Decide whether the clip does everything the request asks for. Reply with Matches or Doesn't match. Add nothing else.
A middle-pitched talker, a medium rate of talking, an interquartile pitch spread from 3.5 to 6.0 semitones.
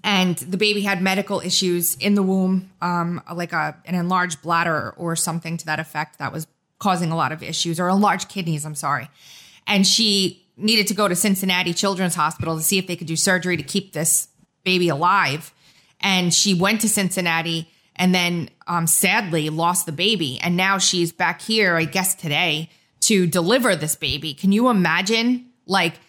Doesn't match